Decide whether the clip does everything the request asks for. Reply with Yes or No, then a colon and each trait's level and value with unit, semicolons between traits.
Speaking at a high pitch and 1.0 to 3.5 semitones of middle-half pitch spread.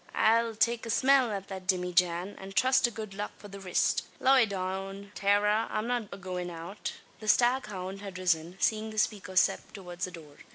Yes: high, 200 Hz; average, 3.0 semitones